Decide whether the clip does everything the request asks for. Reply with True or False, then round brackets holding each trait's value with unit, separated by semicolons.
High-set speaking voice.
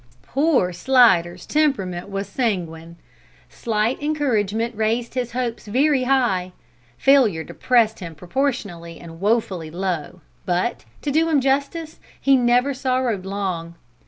True (225 Hz)